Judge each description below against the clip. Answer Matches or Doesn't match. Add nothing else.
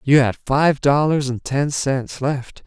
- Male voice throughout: Matches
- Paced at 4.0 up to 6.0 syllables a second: Doesn't match